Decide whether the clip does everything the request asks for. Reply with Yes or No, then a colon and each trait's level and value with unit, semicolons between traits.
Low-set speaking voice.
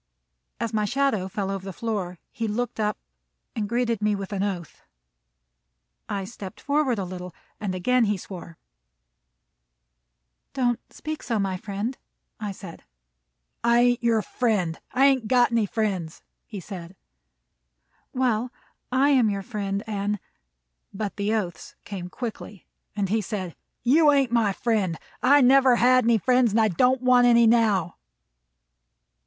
No: high, 215 Hz